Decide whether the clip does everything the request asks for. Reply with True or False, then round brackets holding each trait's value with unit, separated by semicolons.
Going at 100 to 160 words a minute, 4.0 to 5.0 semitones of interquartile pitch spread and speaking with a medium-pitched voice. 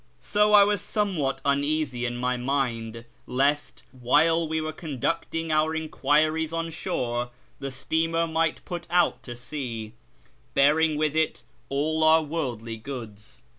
True (140 wpm; 4.3 semitones; 150 Hz)